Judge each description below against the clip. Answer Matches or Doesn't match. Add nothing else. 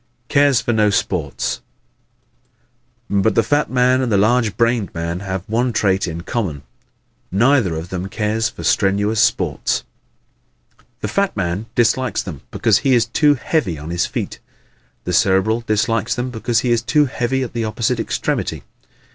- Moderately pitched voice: Doesn't match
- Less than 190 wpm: Matches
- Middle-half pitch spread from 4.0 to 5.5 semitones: Matches